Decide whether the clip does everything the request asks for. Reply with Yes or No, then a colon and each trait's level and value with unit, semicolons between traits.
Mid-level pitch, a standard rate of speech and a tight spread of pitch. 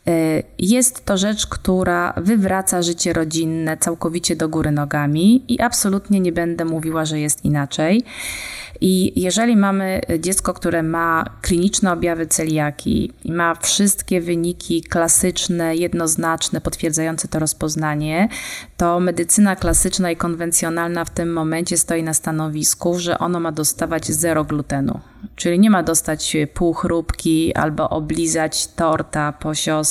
Yes: medium, 170 Hz; average, 130 wpm; narrow, 2.3 semitones